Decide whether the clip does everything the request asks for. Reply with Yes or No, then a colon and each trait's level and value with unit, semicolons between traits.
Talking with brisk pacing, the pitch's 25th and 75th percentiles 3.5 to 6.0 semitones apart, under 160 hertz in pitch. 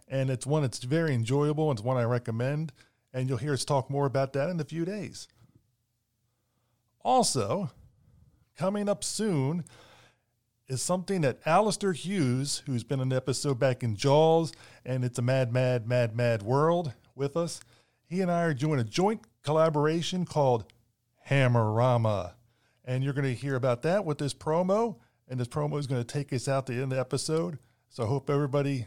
No: average, 185 wpm; average, 4.0 semitones; low, 135 Hz